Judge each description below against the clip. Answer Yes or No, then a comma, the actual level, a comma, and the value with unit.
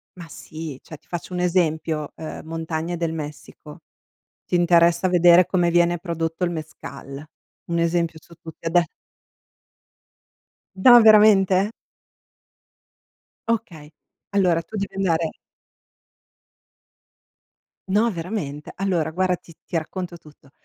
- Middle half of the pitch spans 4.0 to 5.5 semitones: No, narrow, 2.4 semitones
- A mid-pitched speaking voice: Yes, medium, 170 Hz